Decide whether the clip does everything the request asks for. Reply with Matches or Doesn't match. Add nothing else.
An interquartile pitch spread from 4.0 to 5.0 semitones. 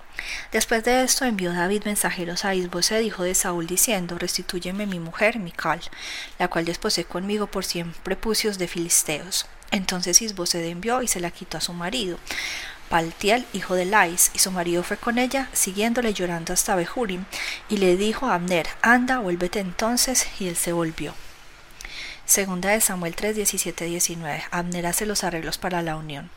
Doesn't match